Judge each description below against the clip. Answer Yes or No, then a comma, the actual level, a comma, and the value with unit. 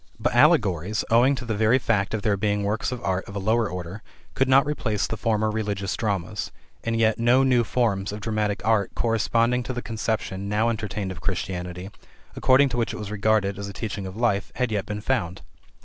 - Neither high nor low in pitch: No, low, 110 Hz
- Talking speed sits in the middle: No, fast, 210 wpm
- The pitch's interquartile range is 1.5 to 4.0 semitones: Yes, narrow, 2.6 semitones